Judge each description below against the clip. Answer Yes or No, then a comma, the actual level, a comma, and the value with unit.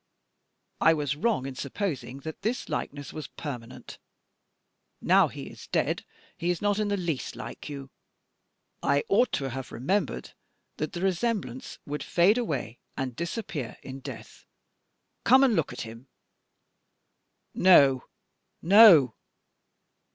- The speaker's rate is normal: No, slow, 130 wpm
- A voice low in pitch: No, medium, 150 Hz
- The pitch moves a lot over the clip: Yes, wide, 6.7 semitones